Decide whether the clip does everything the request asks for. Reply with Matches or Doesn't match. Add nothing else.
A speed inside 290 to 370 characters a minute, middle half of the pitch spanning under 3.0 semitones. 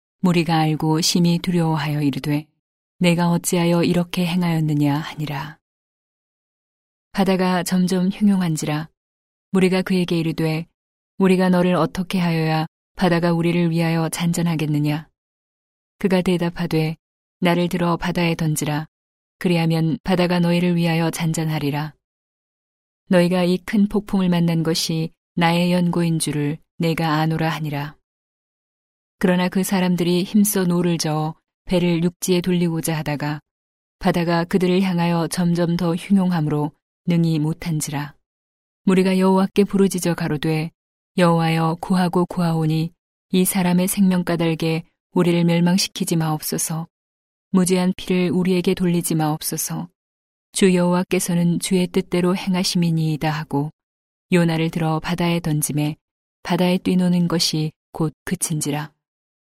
Matches